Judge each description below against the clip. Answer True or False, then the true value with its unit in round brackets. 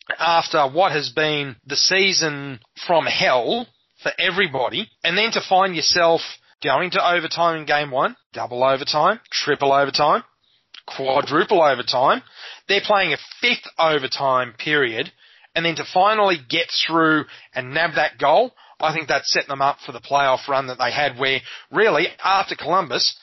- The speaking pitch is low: False (155 Hz)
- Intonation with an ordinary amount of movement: True (3.6 semitones)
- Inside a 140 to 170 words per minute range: True (155 wpm)